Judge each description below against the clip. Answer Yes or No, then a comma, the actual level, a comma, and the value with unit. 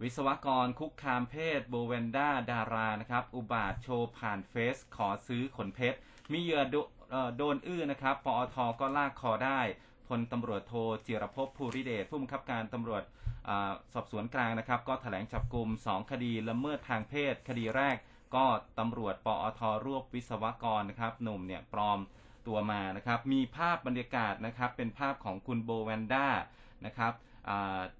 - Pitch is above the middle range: No, low, 120 Hz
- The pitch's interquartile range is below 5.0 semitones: Yes, average, 3.1 semitones